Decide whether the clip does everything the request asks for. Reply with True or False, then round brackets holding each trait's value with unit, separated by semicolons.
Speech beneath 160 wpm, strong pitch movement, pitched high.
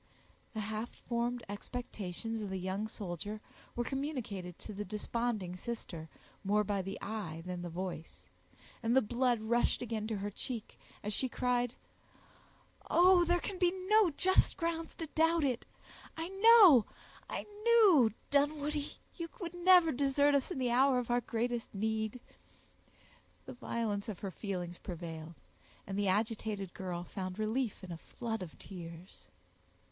True (150 wpm; 5.9 semitones; 225 Hz)